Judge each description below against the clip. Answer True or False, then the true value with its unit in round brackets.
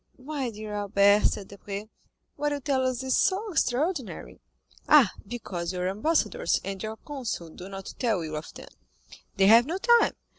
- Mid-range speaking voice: False (220 Hz)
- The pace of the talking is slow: False (160 wpm)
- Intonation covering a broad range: True (6.4 semitones)